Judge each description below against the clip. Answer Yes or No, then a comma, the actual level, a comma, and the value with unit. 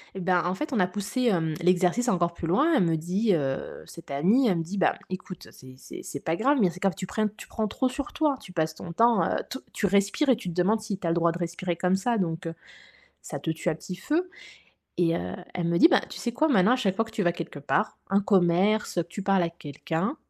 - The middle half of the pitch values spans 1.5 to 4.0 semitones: No, average, 4.4 semitones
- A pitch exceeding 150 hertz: Yes, medium, 185 Hz